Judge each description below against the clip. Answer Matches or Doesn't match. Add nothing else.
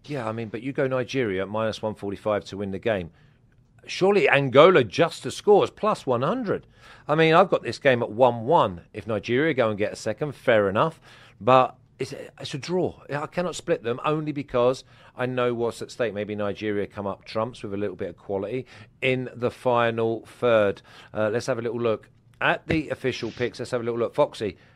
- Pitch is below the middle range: Matches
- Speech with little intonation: Doesn't match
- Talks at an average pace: Doesn't match